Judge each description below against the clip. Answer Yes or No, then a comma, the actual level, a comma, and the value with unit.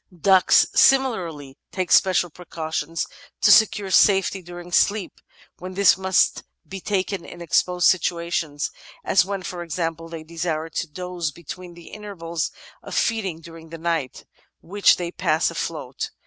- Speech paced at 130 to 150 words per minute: Yes, average, 145 wpm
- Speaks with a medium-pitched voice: Yes, medium, 175 Hz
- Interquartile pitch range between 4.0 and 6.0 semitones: No, narrow, 2.4 semitones